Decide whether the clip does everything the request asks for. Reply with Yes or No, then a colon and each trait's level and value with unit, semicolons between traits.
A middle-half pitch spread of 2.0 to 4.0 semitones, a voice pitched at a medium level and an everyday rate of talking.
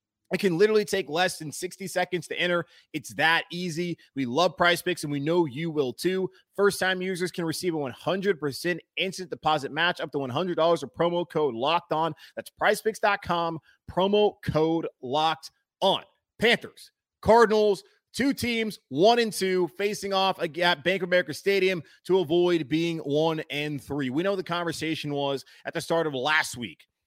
Yes: average, 3.1 semitones; medium, 175 Hz; average, 175 wpm